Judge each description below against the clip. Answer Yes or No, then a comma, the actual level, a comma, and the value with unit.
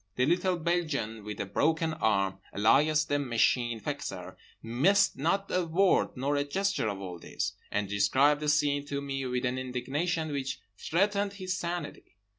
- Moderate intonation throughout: No, wide, 5.8 semitones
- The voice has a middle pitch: Yes, medium, 145 Hz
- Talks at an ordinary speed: Yes, average, 165 wpm